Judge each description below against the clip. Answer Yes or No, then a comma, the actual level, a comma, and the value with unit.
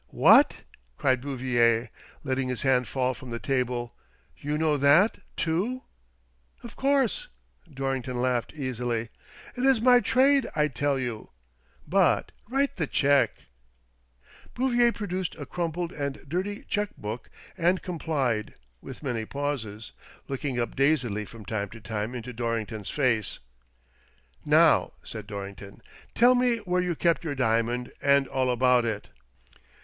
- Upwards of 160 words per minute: No, average, 140 wpm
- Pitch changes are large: Yes, wide, 6.4 semitones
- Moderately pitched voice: No, low, 130 Hz